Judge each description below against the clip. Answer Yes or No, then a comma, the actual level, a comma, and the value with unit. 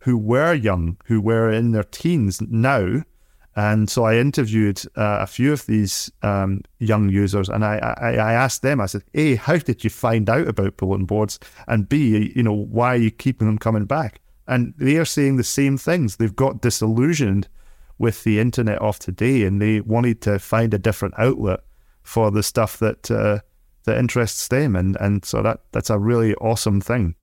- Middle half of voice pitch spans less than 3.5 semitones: Yes, average, 3.0 semitones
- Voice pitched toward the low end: Yes, low, 110 Hz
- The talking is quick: No, average, 195 wpm